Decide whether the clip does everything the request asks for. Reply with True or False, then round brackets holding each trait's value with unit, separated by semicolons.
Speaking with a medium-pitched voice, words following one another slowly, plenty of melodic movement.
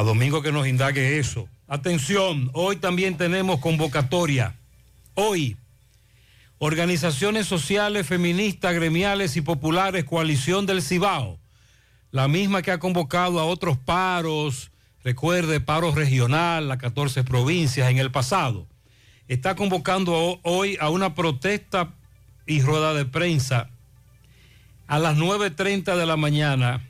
True (155 Hz; 120 wpm; 6.0 semitones)